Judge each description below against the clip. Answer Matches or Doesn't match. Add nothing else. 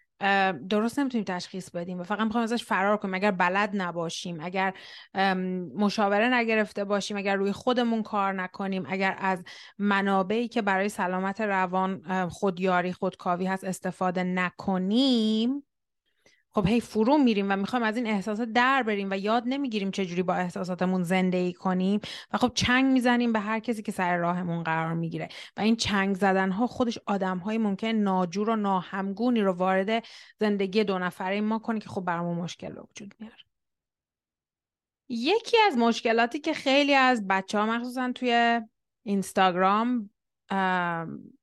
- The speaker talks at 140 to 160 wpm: Matches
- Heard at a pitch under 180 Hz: Doesn't match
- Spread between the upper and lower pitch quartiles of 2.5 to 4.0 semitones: Matches